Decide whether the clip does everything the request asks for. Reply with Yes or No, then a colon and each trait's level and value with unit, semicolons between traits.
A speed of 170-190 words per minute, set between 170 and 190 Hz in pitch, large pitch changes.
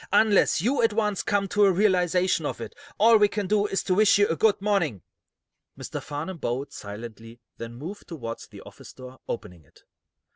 Yes: average, 185 wpm; medium, 185 Hz; wide, 8.4 semitones